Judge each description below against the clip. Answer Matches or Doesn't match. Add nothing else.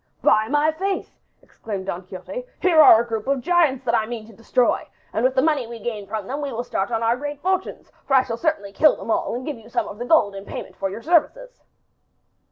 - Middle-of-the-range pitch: Doesn't match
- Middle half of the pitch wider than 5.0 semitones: Matches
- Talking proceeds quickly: Matches